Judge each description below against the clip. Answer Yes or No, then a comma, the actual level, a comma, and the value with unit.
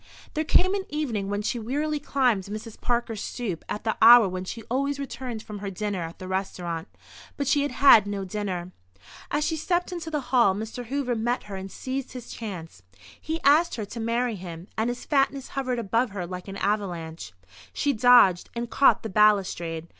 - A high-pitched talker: Yes, high, 225 Hz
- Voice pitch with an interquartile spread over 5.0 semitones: Yes, wide, 5.5 semitones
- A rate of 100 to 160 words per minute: No, average, 195 wpm